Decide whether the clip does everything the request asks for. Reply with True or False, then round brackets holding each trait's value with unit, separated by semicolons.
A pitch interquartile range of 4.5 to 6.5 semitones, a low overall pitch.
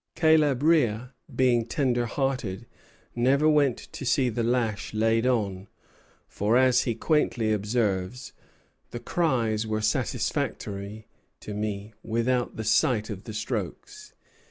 False (3.2 semitones; 115 Hz)